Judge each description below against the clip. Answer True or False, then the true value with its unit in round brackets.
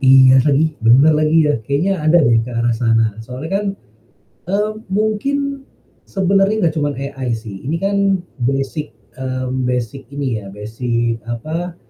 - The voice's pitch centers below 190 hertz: True (135 Hz)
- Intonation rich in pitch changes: True (5.7 semitones)